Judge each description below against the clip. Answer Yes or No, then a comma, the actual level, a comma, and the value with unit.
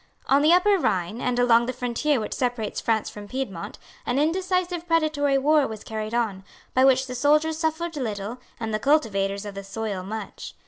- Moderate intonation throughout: No, wide, 6.0 semitones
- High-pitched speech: Yes, very high, 250 Hz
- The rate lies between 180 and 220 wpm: Yes, average, 185 wpm